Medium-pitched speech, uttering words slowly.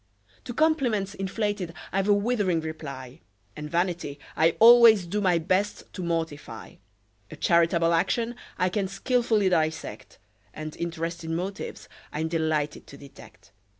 Yes: medium, 175 Hz; slow, 130 wpm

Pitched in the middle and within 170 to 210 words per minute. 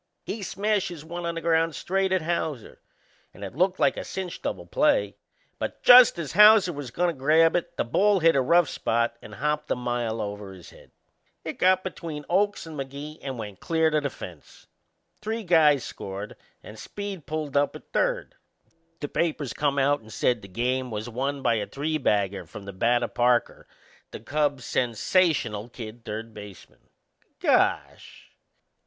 Yes: medium, 145 Hz; average, 180 wpm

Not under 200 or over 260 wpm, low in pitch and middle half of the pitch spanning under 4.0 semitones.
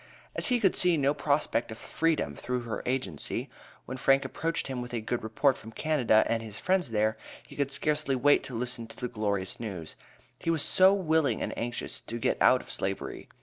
No: fast, 205 wpm; low, 125 Hz; average, 5.1 semitones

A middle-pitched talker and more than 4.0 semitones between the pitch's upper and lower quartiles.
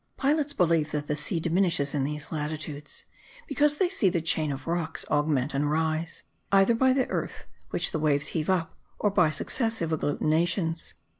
Yes: medium, 160 Hz; average, 4.5 semitones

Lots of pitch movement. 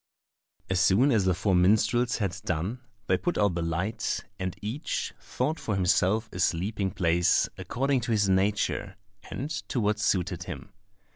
No: average, 3.5 semitones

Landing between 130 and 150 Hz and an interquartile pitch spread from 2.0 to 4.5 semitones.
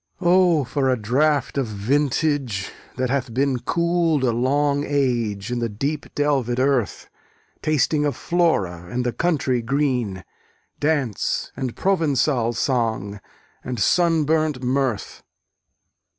Yes: low, 135 Hz; average, 3.8 semitones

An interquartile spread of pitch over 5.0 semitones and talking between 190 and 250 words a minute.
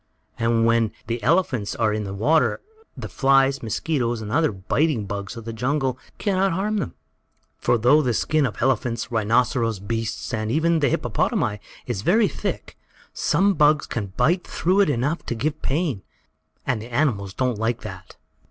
No: wide, 5.6 semitones; average, 170 wpm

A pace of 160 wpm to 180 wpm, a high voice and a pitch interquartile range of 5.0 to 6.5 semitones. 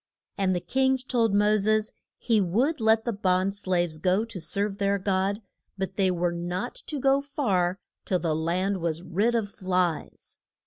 No: average, 175 wpm; high, 195 Hz; average, 3.6 semitones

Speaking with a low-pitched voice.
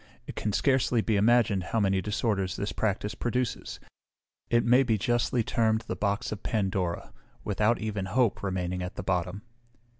Yes: low, 105 Hz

